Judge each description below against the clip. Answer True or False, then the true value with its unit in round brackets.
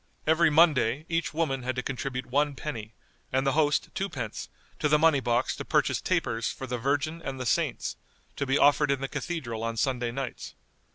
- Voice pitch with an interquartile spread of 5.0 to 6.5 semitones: False (3.5 semitones)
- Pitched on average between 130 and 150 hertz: True (135 Hz)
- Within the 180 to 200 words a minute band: True (190 wpm)